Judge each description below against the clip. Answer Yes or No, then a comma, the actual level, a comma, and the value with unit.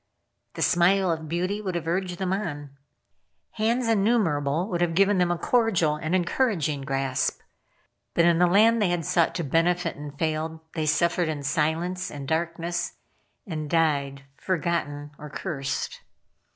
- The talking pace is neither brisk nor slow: Yes, average, 150 wpm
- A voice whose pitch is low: No, medium, 170 Hz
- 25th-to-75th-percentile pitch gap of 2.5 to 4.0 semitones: Yes, average, 3.4 semitones